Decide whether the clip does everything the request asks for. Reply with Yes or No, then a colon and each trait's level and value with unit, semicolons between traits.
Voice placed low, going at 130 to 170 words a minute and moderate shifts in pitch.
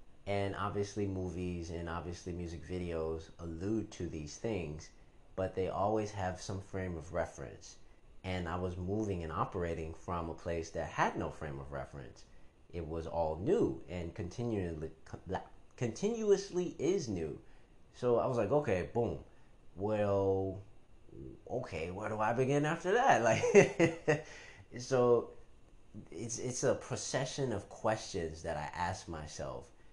Yes: very low, 95 Hz; slow, 135 wpm; average, 4.4 semitones